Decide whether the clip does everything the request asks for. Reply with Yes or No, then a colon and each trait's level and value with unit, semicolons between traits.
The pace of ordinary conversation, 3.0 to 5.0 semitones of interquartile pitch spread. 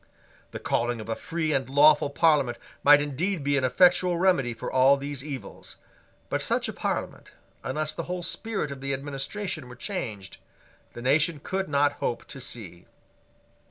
Yes: average, 165 wpm; average, 4.0 semitones